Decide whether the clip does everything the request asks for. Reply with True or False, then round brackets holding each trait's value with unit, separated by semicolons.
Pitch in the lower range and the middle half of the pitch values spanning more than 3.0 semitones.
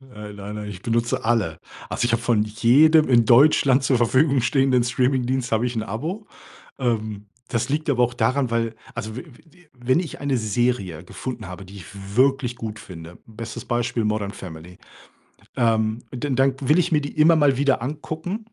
True (120 Hz; 3.8 semitones)